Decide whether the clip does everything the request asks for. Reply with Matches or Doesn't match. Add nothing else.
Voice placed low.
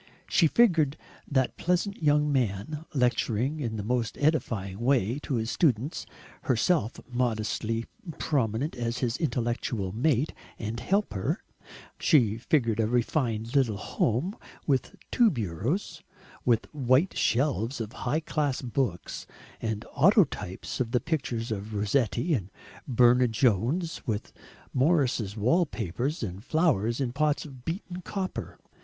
Matches